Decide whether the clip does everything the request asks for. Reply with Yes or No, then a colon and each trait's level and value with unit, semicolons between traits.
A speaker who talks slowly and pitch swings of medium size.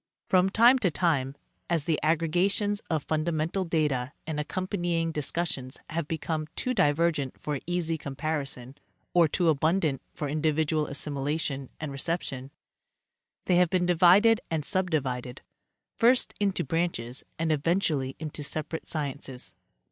Yes: slow, 130 wpm; average, 3.5 semitones